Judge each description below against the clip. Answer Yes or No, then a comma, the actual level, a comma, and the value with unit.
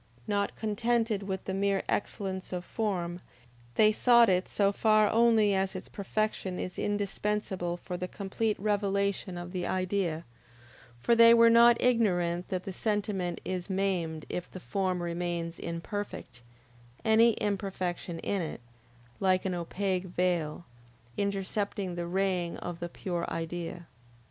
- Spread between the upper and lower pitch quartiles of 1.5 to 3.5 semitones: Yes, average, 2.7 semitones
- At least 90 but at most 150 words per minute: Yes, average, 140 wpm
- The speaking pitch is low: No, high, 190 Hz